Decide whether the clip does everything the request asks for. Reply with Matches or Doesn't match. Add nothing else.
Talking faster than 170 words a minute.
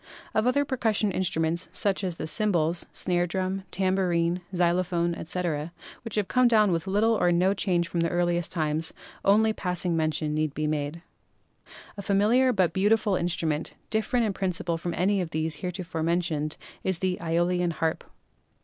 Doesn't match